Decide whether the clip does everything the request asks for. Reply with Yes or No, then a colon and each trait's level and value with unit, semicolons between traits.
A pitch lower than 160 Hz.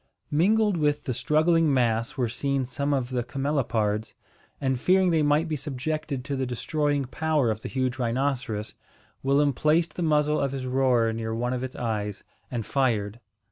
Yes: low, 135 Hz